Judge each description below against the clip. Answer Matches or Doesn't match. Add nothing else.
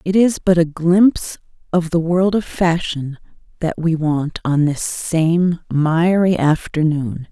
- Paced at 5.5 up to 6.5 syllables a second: Doesn't match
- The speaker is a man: Doesn't match